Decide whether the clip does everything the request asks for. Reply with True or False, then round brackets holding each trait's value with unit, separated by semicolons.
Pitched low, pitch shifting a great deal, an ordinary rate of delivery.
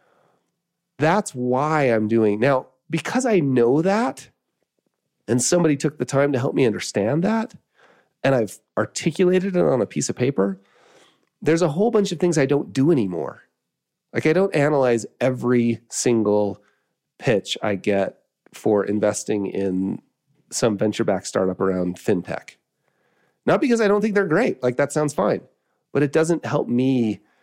True (130 Hz; 7.2 semitones; 160 wpm)